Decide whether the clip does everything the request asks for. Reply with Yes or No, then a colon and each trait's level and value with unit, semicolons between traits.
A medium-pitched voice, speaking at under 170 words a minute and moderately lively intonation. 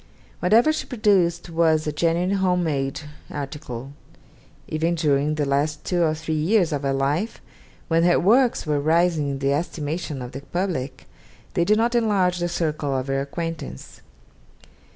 Yes: medium, 160 Hz; average, 160 wpm; average, 3.9 semitones